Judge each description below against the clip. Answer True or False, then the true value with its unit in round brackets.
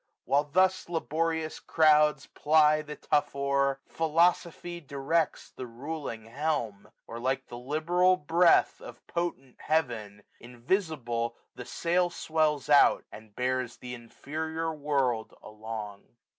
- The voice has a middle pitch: True (145 Hz)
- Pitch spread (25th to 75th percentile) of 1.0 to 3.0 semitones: False (4.7 semitones)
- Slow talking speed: True (115 wpm)